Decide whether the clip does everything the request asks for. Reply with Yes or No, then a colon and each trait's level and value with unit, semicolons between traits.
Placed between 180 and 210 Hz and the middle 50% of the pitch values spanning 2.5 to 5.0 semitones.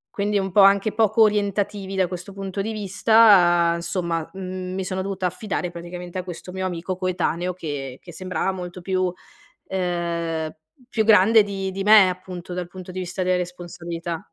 No: medium, 185 Hz; narrow, 2.0 semitones